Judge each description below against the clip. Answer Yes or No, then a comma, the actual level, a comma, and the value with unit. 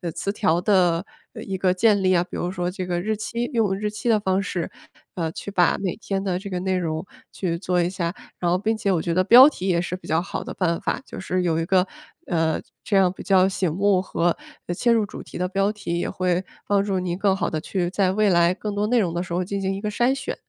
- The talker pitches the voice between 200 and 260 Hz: No, medium, 185 Hz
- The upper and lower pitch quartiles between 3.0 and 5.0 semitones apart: No, narrow, 2.4 semitones